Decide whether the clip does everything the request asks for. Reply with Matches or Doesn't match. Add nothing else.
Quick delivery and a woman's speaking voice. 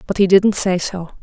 Matches